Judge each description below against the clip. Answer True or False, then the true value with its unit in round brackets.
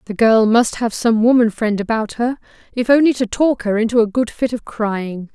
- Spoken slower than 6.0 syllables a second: True (5.0 syllables/s)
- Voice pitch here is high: True (230 Hz)